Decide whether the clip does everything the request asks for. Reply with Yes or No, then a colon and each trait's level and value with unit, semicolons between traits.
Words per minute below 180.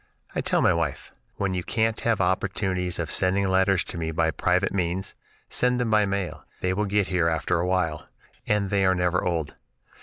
No: average, 185 wpm